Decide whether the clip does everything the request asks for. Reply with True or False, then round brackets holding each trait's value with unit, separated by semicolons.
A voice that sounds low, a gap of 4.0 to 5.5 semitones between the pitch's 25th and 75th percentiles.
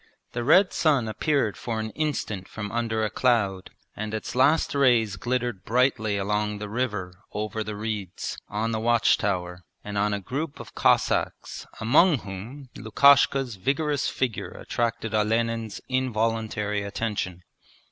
False (110 Hz; 3.4 semitones)